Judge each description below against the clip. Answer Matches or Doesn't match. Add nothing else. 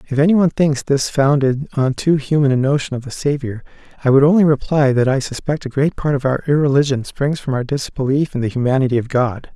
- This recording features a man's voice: Matches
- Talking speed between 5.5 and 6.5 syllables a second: Matches